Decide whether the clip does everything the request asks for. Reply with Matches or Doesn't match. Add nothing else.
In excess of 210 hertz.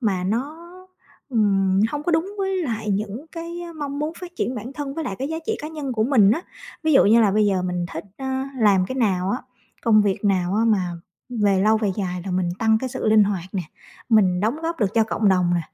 Matches